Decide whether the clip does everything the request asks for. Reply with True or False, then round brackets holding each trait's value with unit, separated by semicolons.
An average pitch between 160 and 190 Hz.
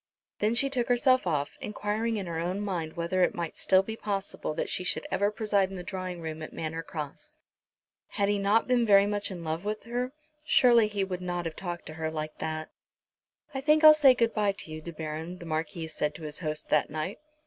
True (185 Hz)